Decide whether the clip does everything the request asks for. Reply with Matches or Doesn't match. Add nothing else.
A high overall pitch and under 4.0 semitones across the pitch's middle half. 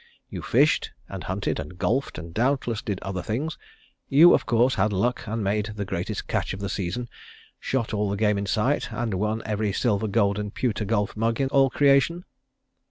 Doesn't match